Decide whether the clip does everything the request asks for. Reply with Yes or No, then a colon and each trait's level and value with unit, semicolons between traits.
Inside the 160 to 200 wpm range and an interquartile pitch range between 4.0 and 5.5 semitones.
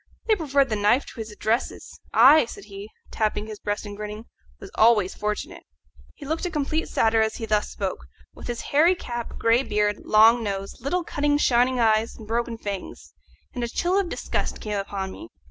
Yes: average, 195 wpm; average, 4.5 semitones